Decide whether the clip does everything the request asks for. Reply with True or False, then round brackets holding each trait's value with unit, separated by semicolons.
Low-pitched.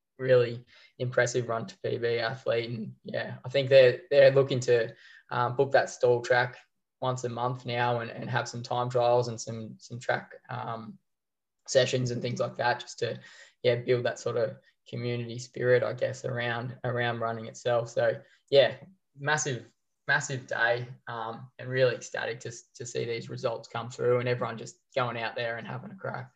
True (120 Hz)